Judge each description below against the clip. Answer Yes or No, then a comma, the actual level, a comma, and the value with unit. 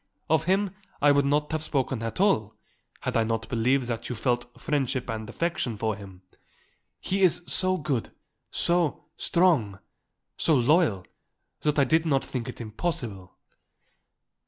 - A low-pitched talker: Yes, low, 130 Hz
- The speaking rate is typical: Yes, average, 150 wpm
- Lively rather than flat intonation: Yes, wide, 6.0 semitones